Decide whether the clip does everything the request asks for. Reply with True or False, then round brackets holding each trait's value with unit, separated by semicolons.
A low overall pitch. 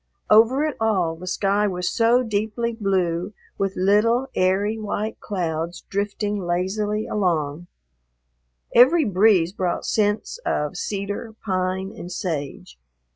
False (200 Hz)